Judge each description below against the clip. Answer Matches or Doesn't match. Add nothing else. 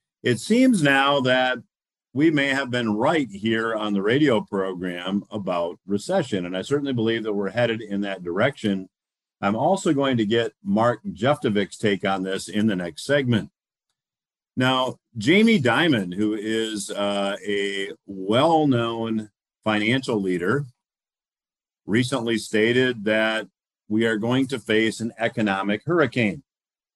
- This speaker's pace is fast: Doesn't match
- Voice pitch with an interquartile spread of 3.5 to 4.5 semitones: Matches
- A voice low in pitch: Matches